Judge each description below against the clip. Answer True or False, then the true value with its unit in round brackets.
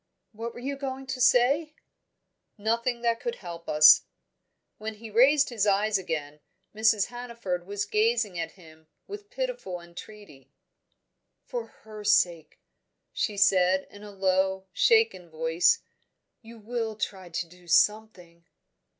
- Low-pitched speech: False (210 Hz)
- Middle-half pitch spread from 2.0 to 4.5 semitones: False (5.1 semitones)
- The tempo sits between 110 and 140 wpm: True (135 wpm)